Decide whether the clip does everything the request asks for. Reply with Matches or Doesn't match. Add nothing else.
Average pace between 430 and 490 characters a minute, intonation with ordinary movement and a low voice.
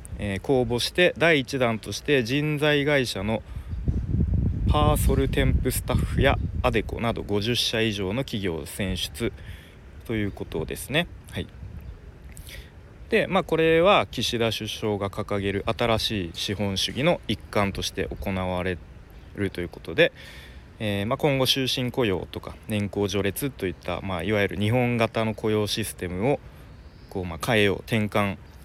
Doesn't match